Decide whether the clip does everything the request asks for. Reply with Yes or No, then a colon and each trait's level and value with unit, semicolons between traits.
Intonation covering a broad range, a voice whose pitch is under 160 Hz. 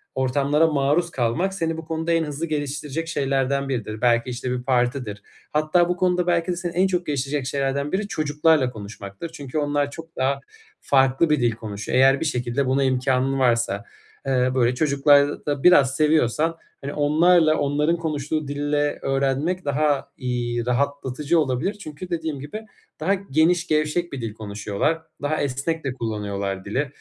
No: average, 3.9 semitones; medium, 140 Hz